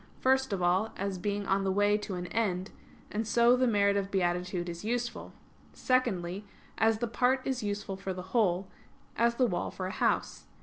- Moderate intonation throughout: Yes, average, 4.0 semitones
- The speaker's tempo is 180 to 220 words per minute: Yes, average, 190 wpm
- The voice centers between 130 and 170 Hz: No, high, 205 Hz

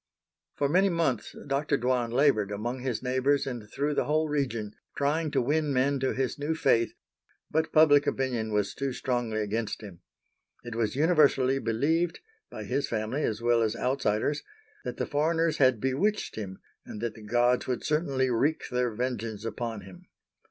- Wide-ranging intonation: No, average, 4.3 semitones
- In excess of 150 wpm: Yes, average, 165 wpm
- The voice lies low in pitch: Yes, low, 130 Hz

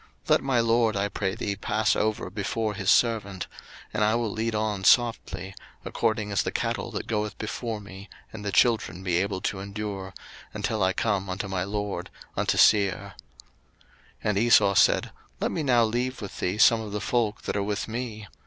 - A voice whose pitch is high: No, low, 105 Hz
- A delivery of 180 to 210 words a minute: Yes, average, 190 wpm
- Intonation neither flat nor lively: No, narrow, 2.2 semitones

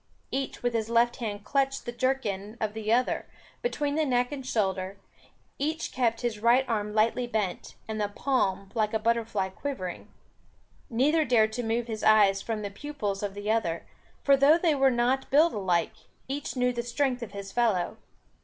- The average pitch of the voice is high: Yes, high, 230 Hz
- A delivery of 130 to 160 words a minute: No, average, 180 wpm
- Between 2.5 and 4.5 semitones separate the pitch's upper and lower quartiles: Yes, average, 4.0 semitones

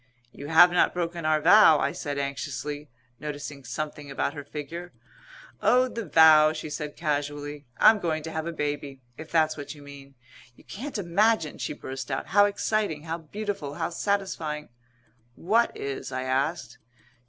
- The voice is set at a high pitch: No, medium, 155 Hz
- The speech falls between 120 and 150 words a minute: No, average, 165 wpm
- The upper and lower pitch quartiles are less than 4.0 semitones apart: Yes, average, 3.2 semitones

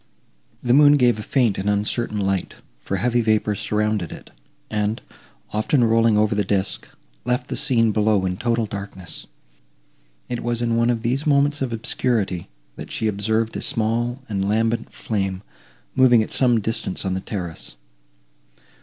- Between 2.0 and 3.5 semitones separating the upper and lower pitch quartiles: Yes, average, 2.8 semitones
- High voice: No, low, 110 Hz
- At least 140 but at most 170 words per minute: Yes, average, 160 wpm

